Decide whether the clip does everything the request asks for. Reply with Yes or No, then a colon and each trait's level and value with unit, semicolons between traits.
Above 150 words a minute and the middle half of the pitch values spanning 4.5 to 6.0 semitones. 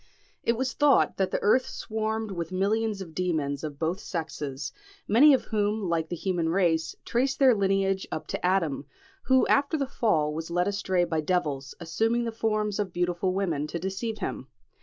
Yes: average, 180 wpm; average, 5.1 semitones